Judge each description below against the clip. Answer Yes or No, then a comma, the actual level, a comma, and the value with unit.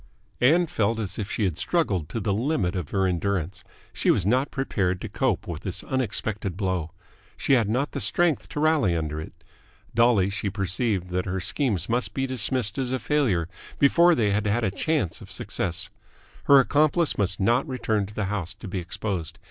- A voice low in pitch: Yes, low, 105 Hz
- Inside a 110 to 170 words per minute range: No, average, 195 wpm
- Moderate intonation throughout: No, wide, 5.8 semitones